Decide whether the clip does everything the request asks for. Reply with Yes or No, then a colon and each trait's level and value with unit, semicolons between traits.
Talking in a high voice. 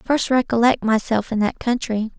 Yes: high, 230 Hz